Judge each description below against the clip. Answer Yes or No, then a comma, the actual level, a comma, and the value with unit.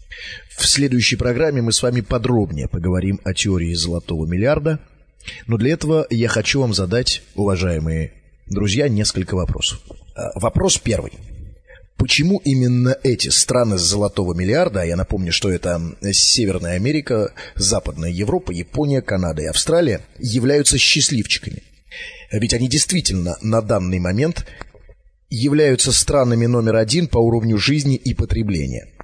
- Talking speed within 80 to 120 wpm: No, average, 130 wpm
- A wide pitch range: Yes, wide, 5.8 semitones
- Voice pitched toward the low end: Yes, low, 110 Hz